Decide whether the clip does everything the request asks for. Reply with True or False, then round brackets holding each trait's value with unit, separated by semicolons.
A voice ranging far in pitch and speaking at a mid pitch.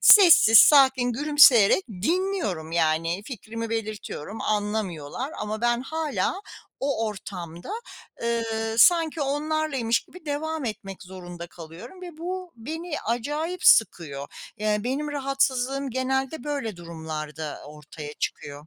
False (8.3 semitones; 230 Hz)